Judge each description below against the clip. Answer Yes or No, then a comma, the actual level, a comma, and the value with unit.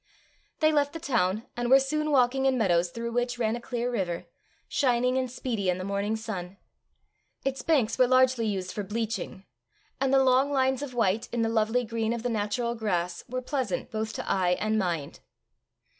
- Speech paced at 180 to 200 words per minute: Yes, average, 190 wpm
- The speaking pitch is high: Yes, high, 235 Hz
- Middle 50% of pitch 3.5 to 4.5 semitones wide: Yes, average, 3.8 semitones